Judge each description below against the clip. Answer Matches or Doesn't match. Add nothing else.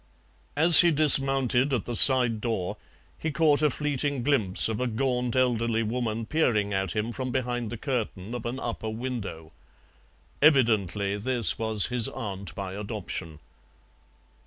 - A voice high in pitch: Doesn't match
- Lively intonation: Doesn't match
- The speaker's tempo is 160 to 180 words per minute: Doesn't match